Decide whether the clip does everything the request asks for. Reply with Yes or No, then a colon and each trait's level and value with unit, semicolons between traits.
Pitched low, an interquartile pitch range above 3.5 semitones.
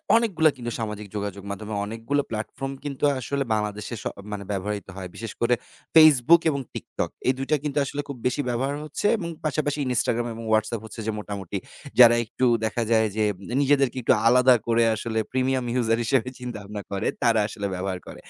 Yes: low, 115 Hz; average, 4.3 semitones